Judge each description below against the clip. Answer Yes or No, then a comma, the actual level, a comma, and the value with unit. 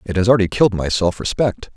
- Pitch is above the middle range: No, low, 100 Hz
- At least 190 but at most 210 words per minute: No, fast, 240 wpm